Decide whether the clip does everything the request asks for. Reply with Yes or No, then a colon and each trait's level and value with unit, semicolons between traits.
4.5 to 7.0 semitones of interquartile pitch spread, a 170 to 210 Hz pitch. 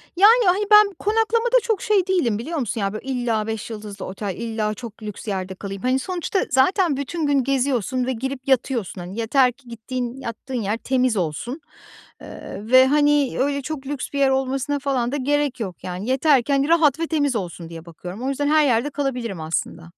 No: average, 4.8 semitones; very high, 260 Hz